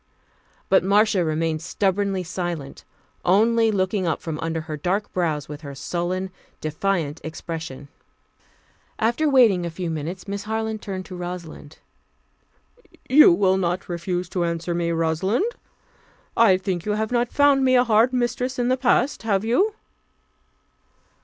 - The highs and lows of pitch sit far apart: No, average, 4.8 semitones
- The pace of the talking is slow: No, average, 145 wpm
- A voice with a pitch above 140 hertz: Yes, medium, 185 Hz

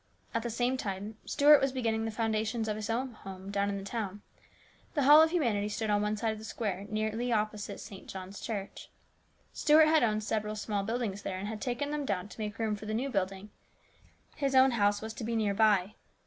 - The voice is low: No, high, 215 Hz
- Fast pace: Yes, fast, 225 wpm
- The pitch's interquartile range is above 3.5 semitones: No, average, 2.7 semitones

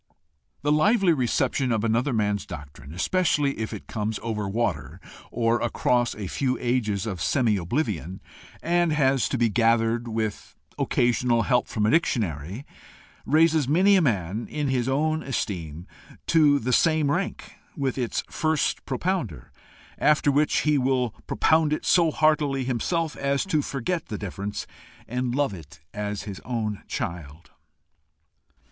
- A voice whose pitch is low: Yes, low, 125 Hz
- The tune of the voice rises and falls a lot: Yes, wide, 5.9 semitones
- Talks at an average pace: Yes, average, 145 wpm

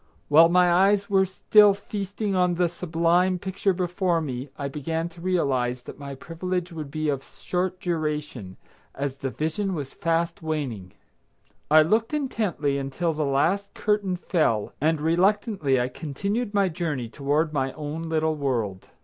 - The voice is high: No, medium, 165 Hz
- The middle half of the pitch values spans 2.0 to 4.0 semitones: No, average, 4.5 semitones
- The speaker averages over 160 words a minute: No, average, 155 wpm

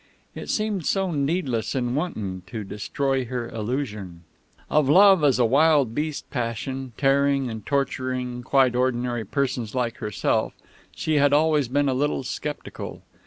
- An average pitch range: Yes, average, 3.4 semitones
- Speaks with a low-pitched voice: Yes, low, 130 Hz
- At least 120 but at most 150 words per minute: Yes, average, 145 wpm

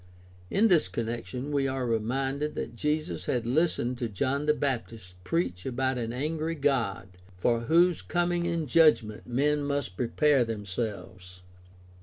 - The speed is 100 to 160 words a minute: Yes, average, 140 wpm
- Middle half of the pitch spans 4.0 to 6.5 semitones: Yes, average, 4.7 semitones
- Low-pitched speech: Yes, low, 130 Hz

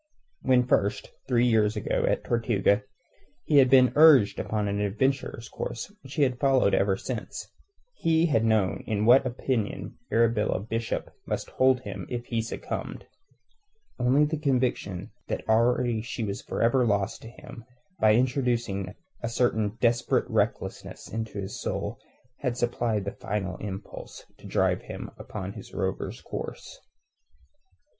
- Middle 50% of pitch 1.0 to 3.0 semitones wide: No, average, 3.4 semitones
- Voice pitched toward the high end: No, low, 115 Hz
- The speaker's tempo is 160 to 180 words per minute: No, average, 145 wpm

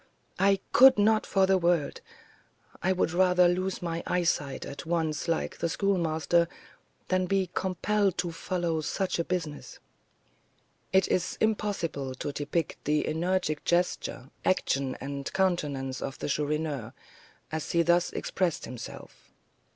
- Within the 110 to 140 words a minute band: Yes, slow, 135 wpm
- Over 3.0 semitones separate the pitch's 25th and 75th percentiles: Yes, average, 3.6 semitones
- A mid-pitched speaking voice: Yes, medium, 170 Hz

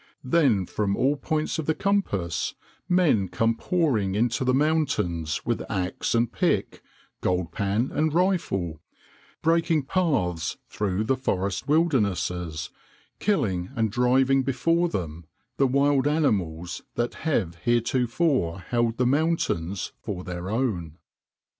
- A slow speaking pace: Yes, slow, 120 wpm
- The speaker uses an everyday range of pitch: No, wide, 8.2 semitones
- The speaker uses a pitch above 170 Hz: No, low, 120 Hz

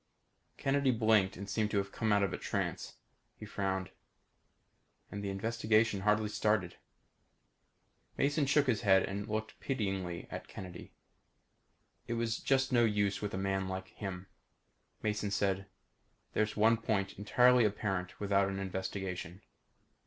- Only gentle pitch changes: Yes, narrow, 2.3 semitones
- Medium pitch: No, low, 100 Hz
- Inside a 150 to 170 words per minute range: No, average, 140 wpm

